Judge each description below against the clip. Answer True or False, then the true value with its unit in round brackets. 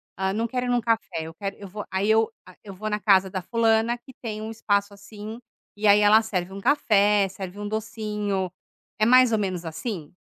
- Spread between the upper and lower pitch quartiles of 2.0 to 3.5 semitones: True (2.5 semitones)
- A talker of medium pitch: False (210 Hz)